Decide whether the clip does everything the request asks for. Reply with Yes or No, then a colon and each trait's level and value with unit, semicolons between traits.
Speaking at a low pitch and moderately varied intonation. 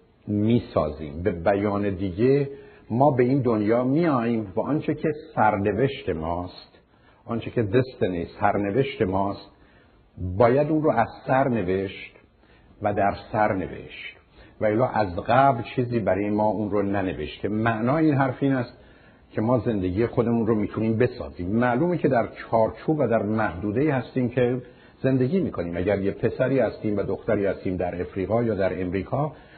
Yes: low, 110 Hz; average, 4.4 semitones